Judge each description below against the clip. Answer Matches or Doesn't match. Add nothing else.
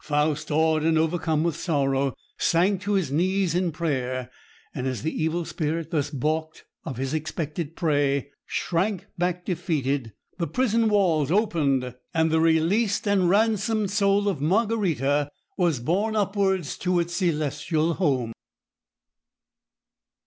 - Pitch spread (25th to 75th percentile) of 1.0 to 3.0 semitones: Doesn't match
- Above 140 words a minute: Doesn't match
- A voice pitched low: Doesn't match